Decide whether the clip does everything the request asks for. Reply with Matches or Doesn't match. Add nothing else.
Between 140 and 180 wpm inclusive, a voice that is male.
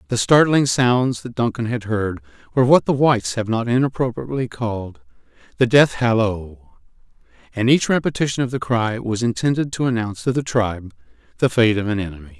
Matches